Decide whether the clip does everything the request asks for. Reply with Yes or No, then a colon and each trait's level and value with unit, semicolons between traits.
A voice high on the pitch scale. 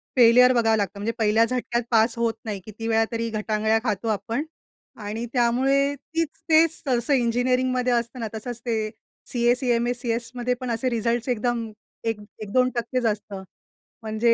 Yes: high, 235 Hz